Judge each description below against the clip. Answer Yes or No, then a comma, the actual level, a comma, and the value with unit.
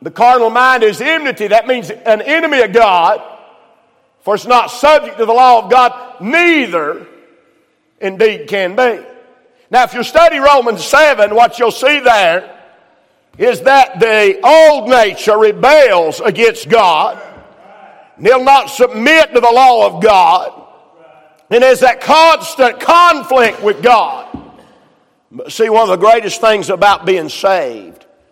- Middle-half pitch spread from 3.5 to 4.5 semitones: Yes, average, 4.1 semitones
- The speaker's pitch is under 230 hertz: No, high, 245 Hz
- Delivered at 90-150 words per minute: Yes, average, 140 wpm